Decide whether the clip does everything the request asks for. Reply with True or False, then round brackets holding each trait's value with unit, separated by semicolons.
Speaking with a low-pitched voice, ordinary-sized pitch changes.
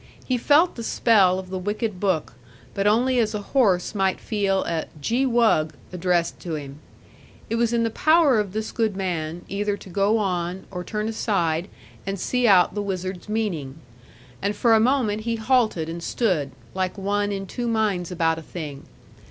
False (200 Hz; 3.9 semitones)